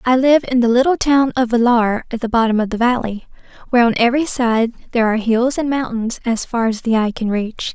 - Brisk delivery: Yes, fast, 230 wpm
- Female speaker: Yes, female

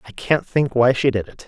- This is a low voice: Yes, low, 125 Hz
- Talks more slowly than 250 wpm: No, fast, 285 wpm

